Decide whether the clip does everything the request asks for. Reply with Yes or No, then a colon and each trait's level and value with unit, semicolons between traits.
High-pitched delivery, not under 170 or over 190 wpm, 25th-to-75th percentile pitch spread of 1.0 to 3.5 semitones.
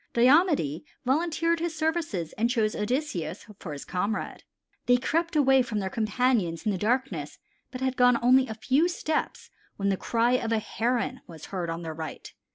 No: high, 240 Hz; average, 175 wpm; wide, 5.5 semitones